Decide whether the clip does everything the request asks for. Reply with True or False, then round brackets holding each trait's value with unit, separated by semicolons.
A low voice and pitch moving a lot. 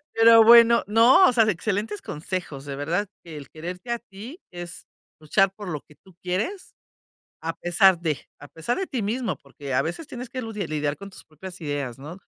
False (185 Hz; 6.6 semitones)